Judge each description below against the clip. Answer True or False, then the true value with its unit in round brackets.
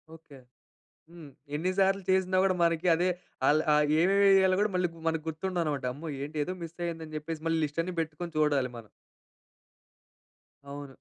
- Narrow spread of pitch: False (3.4 semitones)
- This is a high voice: False (165 Hz)